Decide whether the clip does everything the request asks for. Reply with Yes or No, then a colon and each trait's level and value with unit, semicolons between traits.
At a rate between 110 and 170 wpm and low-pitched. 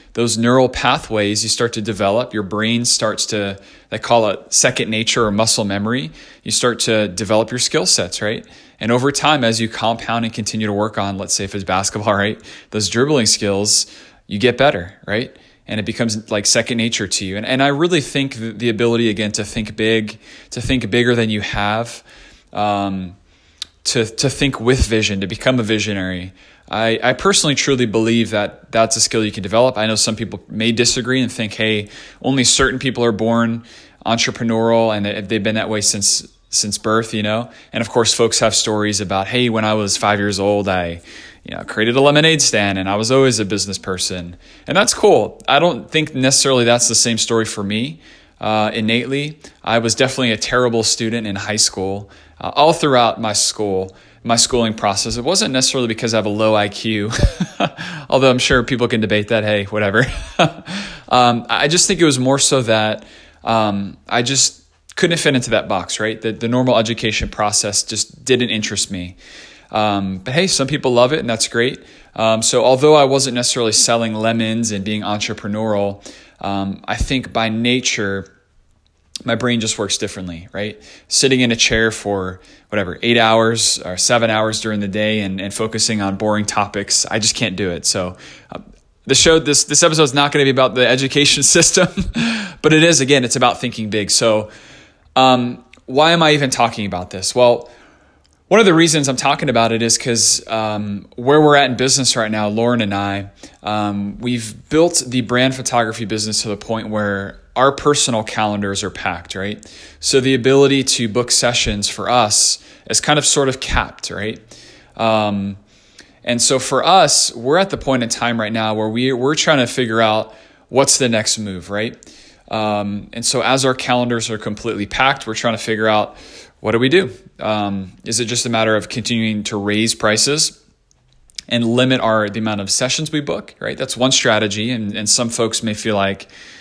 No: average, 195 wpm; low, 115 Hz